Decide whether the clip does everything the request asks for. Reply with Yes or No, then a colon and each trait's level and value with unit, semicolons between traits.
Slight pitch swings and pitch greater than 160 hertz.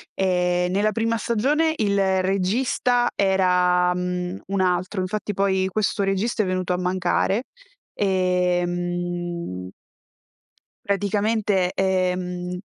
Yes: narrow, 2.2 semitones; medium, 185 Hz